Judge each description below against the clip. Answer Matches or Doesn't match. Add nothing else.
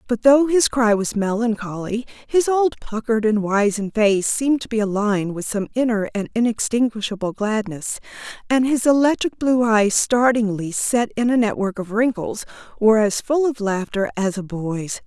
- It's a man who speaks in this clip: Doesn't match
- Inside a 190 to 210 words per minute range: Doesn't match